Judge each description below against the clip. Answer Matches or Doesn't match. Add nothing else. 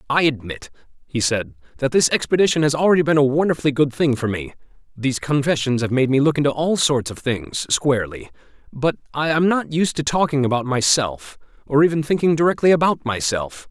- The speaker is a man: Matches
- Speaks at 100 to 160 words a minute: Doesn't match